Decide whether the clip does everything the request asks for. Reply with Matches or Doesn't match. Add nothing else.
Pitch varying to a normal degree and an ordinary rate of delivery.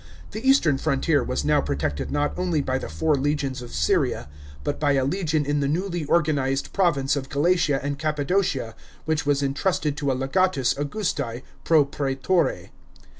Matches